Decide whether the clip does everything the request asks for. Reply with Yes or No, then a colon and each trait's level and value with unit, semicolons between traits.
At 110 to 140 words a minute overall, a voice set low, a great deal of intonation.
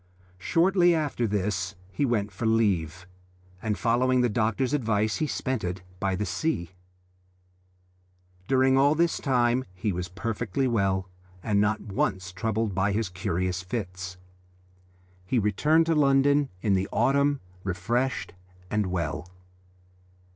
Yes: slow, 135 wpm; low, 110 Hz; wide, 5.8 semitones